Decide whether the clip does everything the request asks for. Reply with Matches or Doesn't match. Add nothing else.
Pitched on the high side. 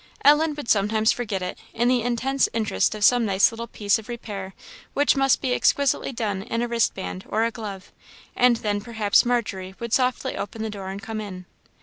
Matches